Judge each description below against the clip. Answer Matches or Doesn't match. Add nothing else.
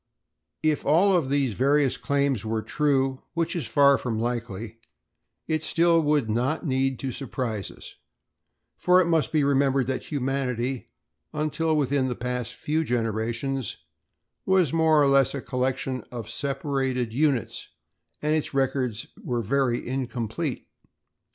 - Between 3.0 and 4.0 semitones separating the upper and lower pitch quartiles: Matches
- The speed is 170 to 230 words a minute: Doesn't match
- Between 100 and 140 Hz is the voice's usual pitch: Matches